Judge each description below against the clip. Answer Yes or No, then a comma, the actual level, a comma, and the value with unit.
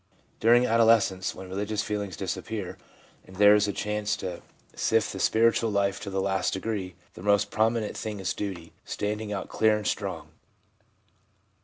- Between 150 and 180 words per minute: Yes, average, 165 wpm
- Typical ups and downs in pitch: No, narrow, 2.2 semitones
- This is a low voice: Yes, low, 105 Hz